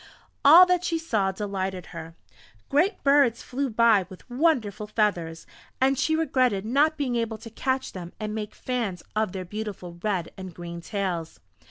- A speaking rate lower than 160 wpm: No, average, 165 wpm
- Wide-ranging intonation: Yes, wide, 5.8 semitones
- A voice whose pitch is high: Yes, high, 215 Hz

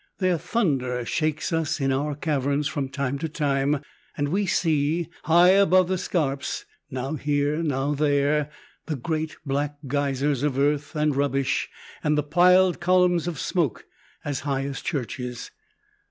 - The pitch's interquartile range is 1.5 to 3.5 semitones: Yes, average, 2.8 semitones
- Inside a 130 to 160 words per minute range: Yes, average, 150 wpm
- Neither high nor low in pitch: Yes, medium, 145 Hz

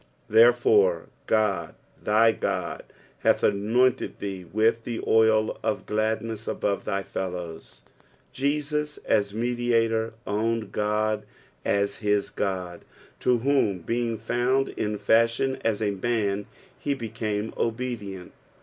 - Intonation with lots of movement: No, narrow, 2.5 semitones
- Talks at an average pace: No, slow, 115 wpm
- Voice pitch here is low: Yes, low, 110 Hz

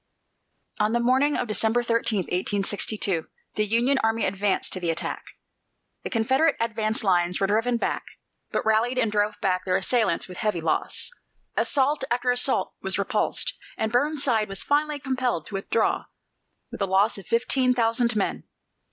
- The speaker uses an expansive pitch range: No, average, 3.9 semitones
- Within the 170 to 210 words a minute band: No, average, 160 wpm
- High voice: Yes, high, 220 Hz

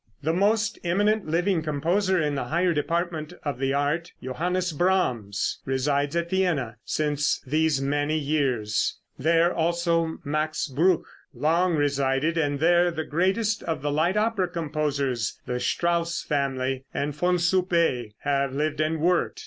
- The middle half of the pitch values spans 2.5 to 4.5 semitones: Yes, average, 3.5 semitones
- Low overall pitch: No, medium, 155 Hz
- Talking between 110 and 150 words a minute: Yes, average, 140 wpm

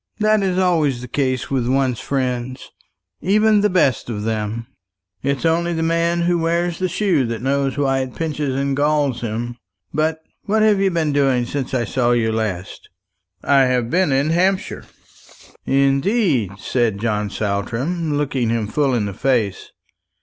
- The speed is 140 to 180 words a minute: Yes, average, 165 wpm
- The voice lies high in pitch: No, low, 135 Hz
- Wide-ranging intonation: Yes, wide, 5.7 semitones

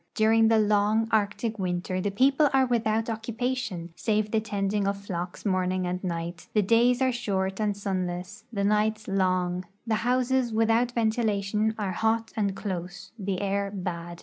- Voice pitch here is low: No, high, 205 Hz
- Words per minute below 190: Yes, average, 160 wpm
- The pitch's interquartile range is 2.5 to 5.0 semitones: Yes, average, 3.2 semitones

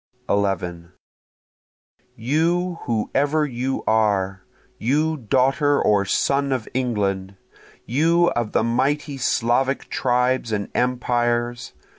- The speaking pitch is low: Yes, low, 125 Hz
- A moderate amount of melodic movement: Yes, average, 4.4 semitones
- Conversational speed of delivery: No, slow, 95 wpm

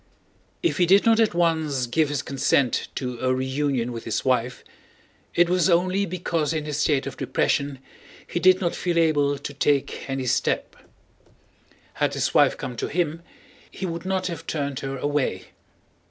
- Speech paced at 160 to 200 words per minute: Yes, average, 170 wpm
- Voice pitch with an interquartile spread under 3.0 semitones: No, average, 4.4 semitones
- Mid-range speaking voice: Yes, medium, 150 Hz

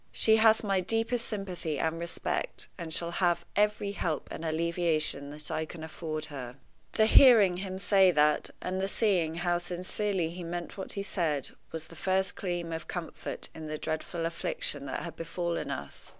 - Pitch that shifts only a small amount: No, average, 3.2 semitones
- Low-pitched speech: No, medium, 175 Hz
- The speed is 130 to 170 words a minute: No, average, 180 wpm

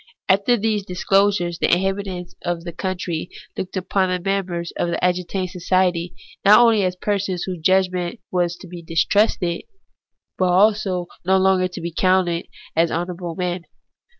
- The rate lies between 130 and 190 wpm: Yes, average, 155 wpm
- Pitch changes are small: Yes, narrow, 1.8 semitones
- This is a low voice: No, medium, 180 Hz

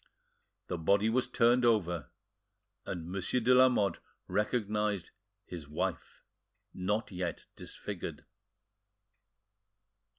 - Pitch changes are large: No, average, 4.5 semitones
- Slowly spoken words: Yes, slow, 90 wpm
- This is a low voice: Yes, low, 100 Hz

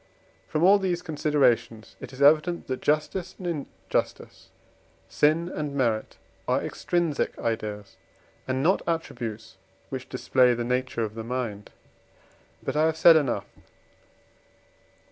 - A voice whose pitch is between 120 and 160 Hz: Yes, low, 135 Hz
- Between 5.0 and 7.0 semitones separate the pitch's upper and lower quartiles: Yes, wide, 5.4 semitones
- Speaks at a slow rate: Yes, slow, 125 wpm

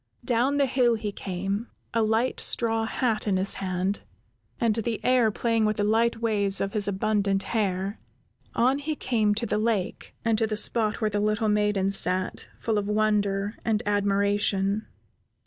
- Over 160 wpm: Yes, average, 170 wpm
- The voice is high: Yes, high, 215 Hz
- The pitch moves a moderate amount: No, narrow, 2.2 semitones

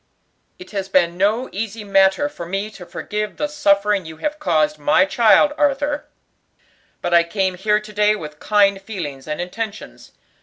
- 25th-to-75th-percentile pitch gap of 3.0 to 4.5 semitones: Yes, average, 3.6 semitones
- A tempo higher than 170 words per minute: No, average, 165 wpm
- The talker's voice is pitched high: Yes, high, 200 Hz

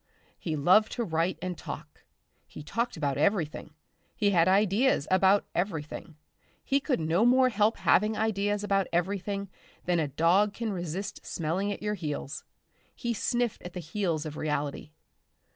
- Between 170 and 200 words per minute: No, average, 155 wpm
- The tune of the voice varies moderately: Yes, average, 4.4 semitones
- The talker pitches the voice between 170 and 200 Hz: Yes, high, 190 Hz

